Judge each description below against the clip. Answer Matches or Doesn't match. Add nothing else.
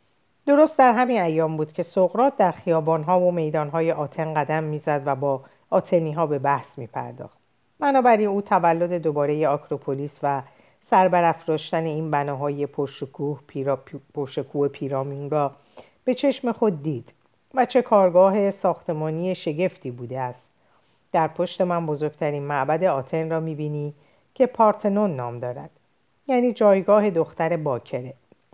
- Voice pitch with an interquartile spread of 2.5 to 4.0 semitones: Doesn't match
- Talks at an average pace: Matches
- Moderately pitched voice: Matches